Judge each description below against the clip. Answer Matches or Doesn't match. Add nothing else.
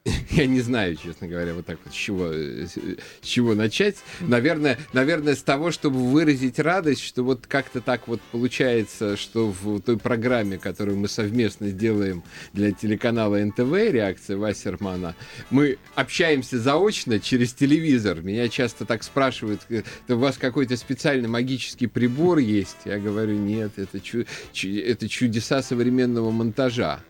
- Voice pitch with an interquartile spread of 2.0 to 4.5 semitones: Matches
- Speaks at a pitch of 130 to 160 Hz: Doesn't match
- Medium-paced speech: Matches